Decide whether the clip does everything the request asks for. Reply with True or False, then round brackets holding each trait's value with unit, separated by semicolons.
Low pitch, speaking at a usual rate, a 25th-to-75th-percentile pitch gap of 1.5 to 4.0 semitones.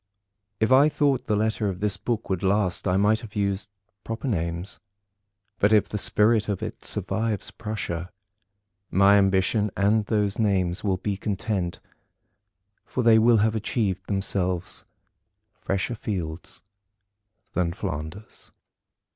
False (100 Hz; 130 wpm; 2.6 semitones)